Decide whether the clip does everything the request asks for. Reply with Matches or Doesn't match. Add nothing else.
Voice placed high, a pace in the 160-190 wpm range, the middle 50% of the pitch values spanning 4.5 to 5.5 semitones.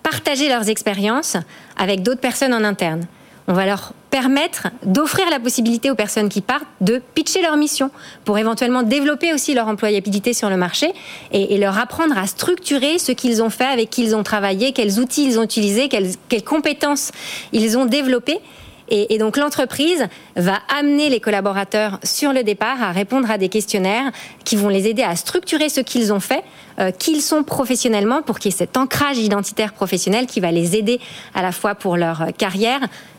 Matches